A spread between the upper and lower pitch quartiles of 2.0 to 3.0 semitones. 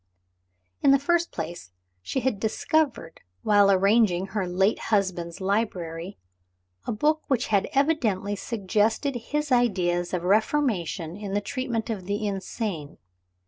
No: average, 4.8 semitones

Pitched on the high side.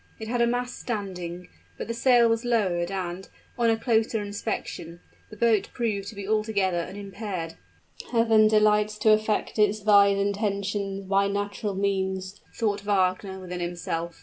Yes: high, 205 Hz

